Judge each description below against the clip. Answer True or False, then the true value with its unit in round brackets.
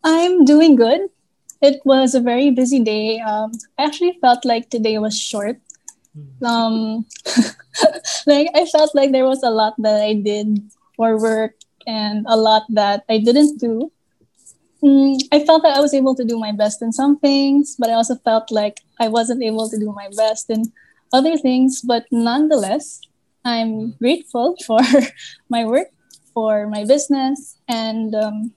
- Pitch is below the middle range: False (240 Hz)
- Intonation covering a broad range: False (4.2 semitones)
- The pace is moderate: True (165 wpm)